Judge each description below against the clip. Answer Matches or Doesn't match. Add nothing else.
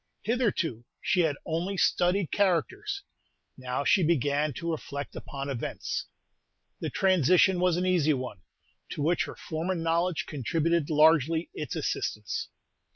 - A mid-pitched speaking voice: Matches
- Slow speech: Matches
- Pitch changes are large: Doesn't match